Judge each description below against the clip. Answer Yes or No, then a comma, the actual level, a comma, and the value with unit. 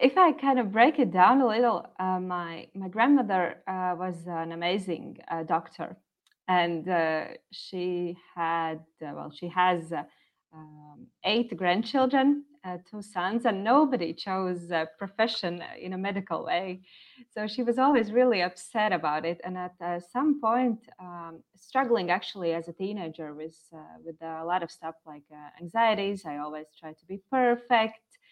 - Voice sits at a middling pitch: Yes, medium, 180 Hz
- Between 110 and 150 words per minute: No, average, 165 wpm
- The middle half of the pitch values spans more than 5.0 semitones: Yes, wide, 5.6 semitones